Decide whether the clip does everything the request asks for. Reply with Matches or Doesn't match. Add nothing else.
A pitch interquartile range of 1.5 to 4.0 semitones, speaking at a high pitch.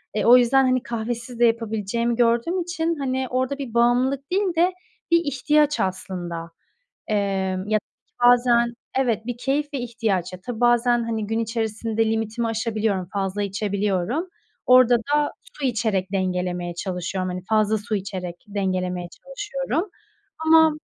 Doesn't match